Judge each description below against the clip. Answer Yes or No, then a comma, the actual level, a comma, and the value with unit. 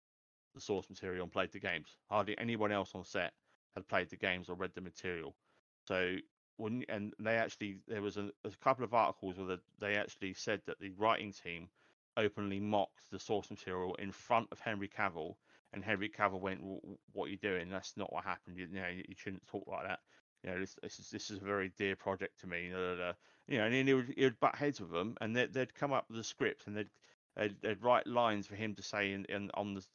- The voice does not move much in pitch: Yes, narrow, 2.0 semitones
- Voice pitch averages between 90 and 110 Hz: Yes, low, 100 Hz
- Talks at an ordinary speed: No, fast, 240 wpm